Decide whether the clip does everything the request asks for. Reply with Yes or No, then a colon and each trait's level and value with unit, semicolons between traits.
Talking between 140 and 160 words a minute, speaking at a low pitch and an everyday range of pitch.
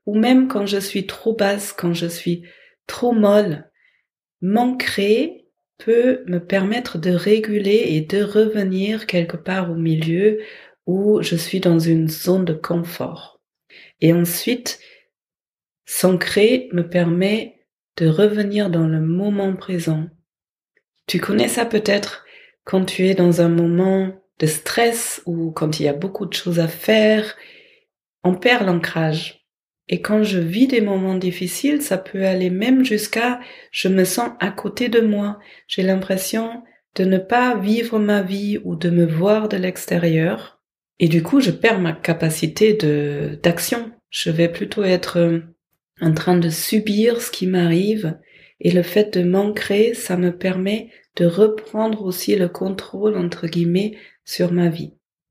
No: average, 150 wpm; high, 190 Hz; average, 3.9 semitones